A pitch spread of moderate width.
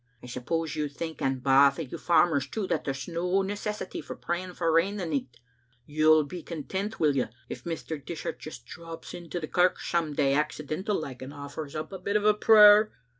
Yes: average, 4.0 semitones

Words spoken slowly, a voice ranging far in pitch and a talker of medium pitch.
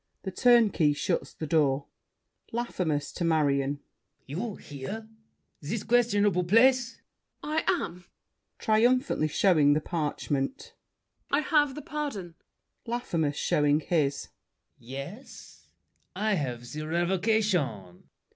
Yes: slow, 105 wpm; wide, 7.8 semitones; medium, 175 Hz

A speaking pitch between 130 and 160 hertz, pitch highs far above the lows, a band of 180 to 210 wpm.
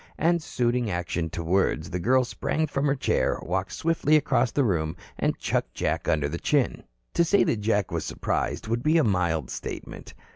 No: low, 115 Hz; wide, 8.6 semitones; average, 190 wpm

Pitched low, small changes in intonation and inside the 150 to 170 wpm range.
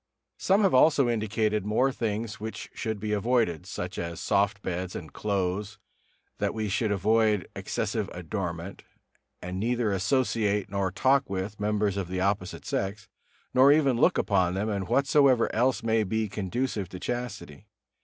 No: low, 105 Hz; average, 3.3 semitones; average, 155 wpm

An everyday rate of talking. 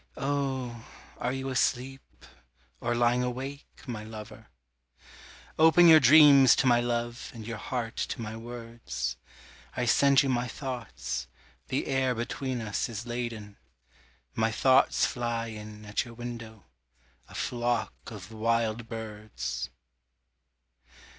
No: slow, 125 wpm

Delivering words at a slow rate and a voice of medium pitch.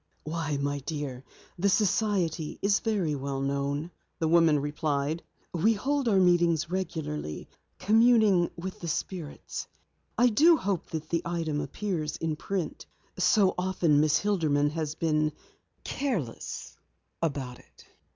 Yes: slow, 130 wpm; medium, 165 Hz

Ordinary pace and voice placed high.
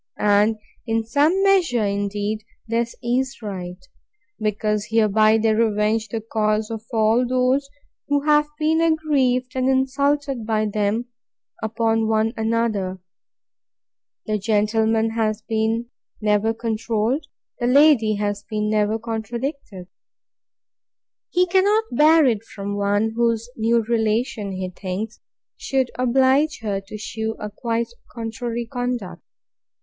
No: slow, 120 wpm; high, 225 Hz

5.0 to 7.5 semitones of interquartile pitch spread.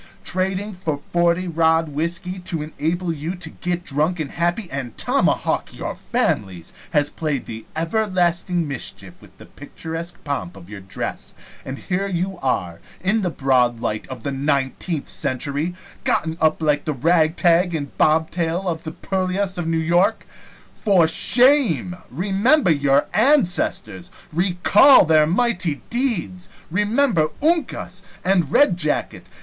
No: average, 4.0 semitones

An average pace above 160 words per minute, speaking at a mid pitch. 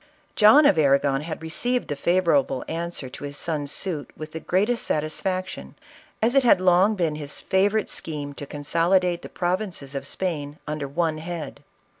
Yes: average, 170 wpm; medium, 165 Hz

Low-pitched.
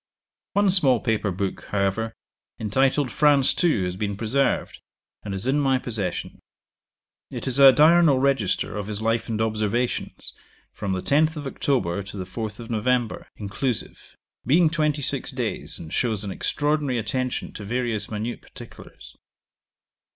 Yes: low, 115 Hz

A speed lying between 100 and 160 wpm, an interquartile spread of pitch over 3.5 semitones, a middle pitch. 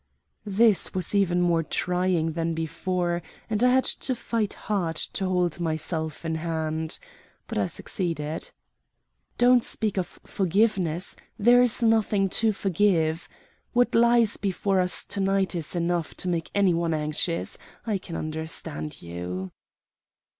Yes: average, 140 wpm; average, 4.0 semitones; medium, 180 Hz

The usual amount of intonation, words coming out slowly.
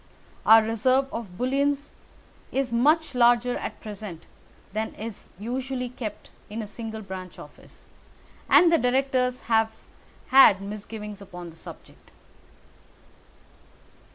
Yes: average, 3.4 semitones; slow, 115 wpm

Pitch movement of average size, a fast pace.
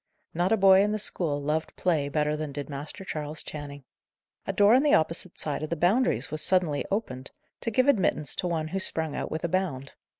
Yes: average, 4.4 semitones; fast, 220 wpm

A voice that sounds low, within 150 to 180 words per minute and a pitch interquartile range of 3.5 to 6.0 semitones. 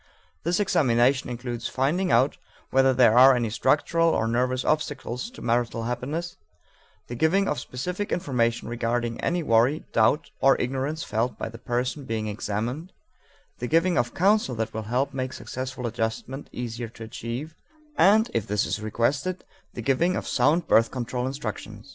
Yes: low, 125 Hz; average, 160 wpm; average, 4.6 semitones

